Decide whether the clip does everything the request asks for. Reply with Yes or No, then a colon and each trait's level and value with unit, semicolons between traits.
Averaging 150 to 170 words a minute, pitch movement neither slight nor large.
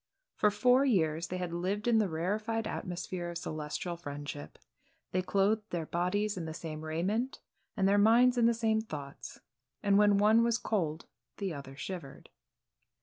Yes: average, 165 wpm; average, 4.9 semitones